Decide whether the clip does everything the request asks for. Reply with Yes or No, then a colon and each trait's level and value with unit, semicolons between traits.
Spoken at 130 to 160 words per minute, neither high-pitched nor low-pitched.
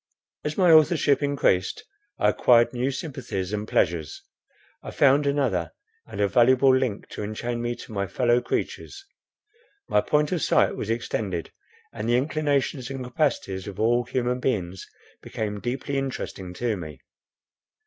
No: average, 150 wpm; low, 120 Hz